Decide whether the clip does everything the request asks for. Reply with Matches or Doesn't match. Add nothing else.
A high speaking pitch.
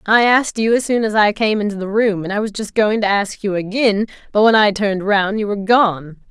Matches